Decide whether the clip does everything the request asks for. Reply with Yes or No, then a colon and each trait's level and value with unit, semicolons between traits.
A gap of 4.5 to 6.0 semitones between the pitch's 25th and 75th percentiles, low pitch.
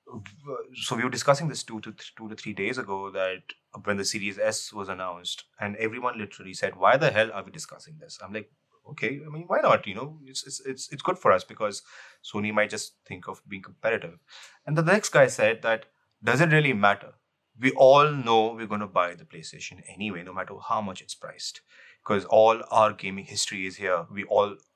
Yes: average, 5.3 semitones; low, 110 Hz